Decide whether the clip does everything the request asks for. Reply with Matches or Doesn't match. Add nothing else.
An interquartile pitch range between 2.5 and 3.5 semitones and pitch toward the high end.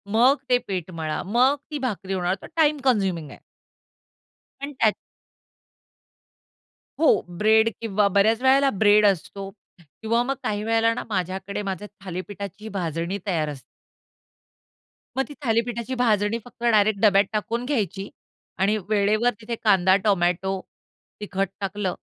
Matches